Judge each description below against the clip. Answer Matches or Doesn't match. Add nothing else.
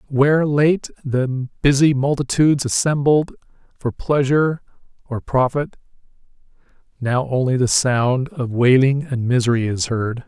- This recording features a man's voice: Matches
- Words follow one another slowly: Matches